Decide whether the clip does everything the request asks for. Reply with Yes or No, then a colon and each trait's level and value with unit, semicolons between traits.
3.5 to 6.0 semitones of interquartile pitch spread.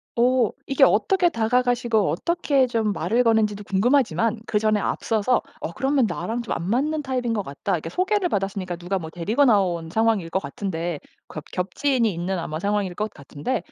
Yes: wide, 5.4 semitones